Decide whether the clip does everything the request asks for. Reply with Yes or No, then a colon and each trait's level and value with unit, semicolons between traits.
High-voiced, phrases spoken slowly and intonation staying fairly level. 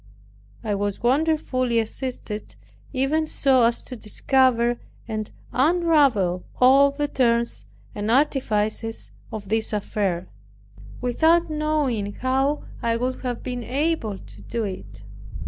No: high, 245 Hz; slow, 115 wpm; average, 4.3 semitones